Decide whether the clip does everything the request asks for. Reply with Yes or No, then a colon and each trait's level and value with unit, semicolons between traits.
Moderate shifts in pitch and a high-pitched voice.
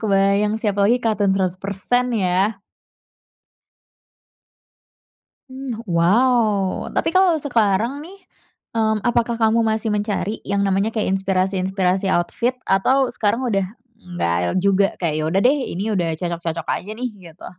Yes: average, 3.5 semitones; high, 200 Hz